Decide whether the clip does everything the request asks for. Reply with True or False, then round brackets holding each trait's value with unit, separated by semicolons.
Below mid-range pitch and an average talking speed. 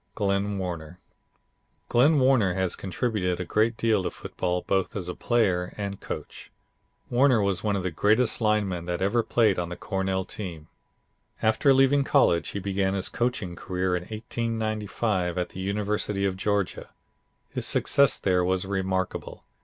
True (100 Hz; 155 wpm)